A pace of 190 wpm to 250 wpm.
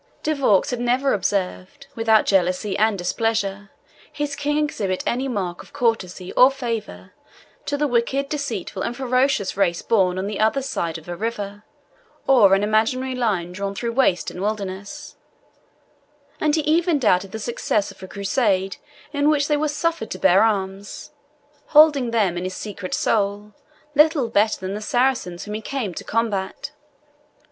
No: average, 165 wpm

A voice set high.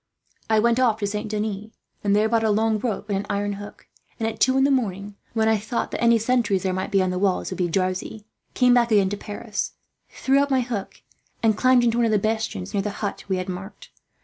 Yes: high, 215 Hz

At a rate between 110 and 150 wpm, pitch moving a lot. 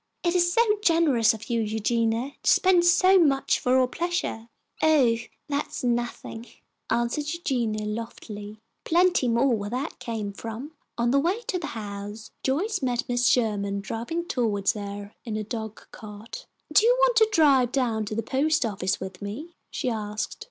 No: average, 165 wpm; wide, 6.4 semitones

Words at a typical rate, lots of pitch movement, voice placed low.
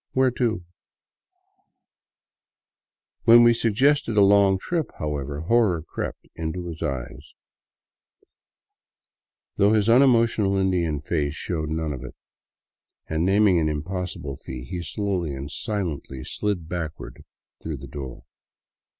No: slow, 120 wpm; wide, 5.7 semitones; very low, 90 Hz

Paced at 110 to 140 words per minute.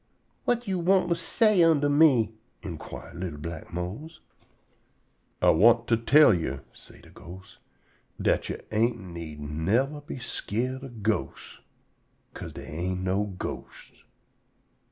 Yes: slow, 135 wpm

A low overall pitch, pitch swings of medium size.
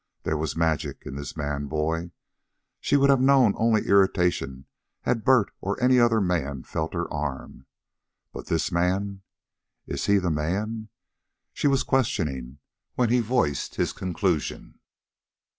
No: very low, 90 Hz; wide, 6.8 semitones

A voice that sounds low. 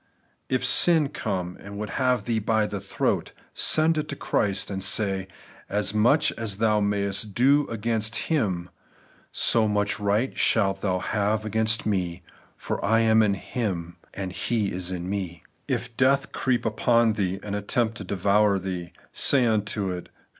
Yes: low, 105 Hz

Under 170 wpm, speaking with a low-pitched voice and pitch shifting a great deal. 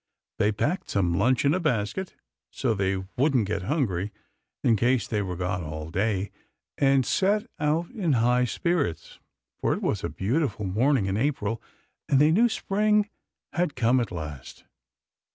Yes: average, 160 wpm; low, 125 Hz; wide, 7.5 semitones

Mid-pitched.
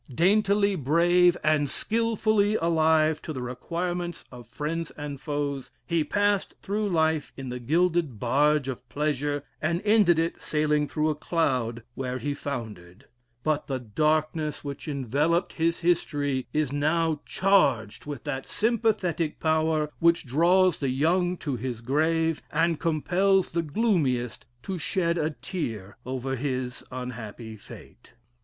Yes: medium, 155 Hz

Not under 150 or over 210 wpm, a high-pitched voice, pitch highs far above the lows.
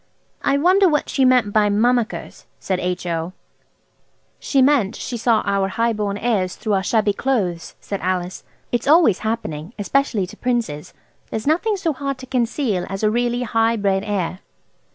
No: average, 165 wpm; high, 220 Hz; average, 4.7 semitones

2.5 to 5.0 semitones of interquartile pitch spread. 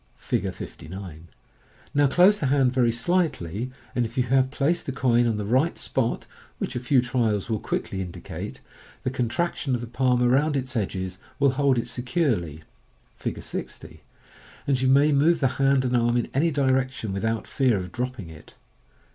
Yes: average, 3.3 semitones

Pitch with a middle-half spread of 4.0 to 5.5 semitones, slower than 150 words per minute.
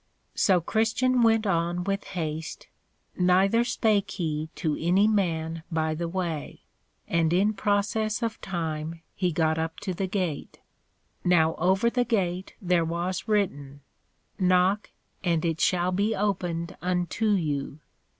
No: average, 3.6 semitones; slow, 135 wpm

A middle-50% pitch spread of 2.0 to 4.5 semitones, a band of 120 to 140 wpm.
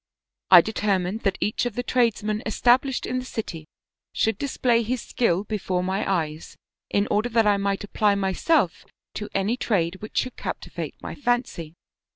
No: average, 4.0 semitones; average, 165 wpm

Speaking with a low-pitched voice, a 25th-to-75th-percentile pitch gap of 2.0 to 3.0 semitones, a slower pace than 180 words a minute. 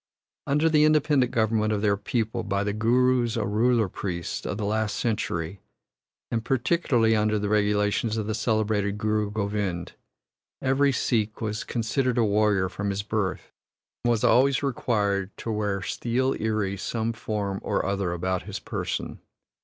Yes: low, 110 Hz; average, 2.7 semitones; average, 155 wpm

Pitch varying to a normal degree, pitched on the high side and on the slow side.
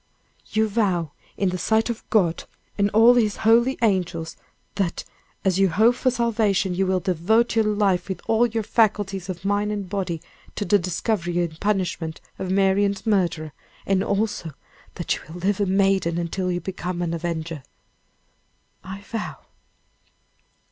No: average, 3.3 semitones; high, 195 Hz; average, 155 wpm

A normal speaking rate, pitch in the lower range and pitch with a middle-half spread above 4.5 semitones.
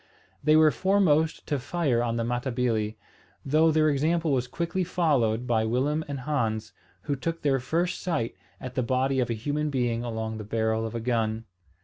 Yes: average, 185 wpm; low, 130 Hz; average, 5.0 semitones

